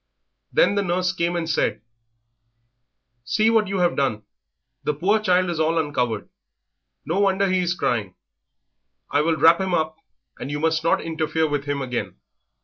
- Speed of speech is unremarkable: Yes, average, 165 wpm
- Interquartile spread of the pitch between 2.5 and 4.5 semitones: Yes, average, 3.9 semitones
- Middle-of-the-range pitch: Yes, medium, 165 Hz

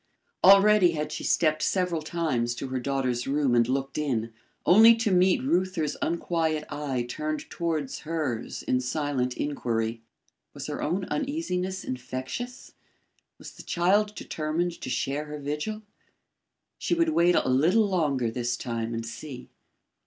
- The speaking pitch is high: No, medium, 150 Hz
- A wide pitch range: Yes, wide, 5.9 semitones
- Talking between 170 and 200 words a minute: No, average, 145 wpm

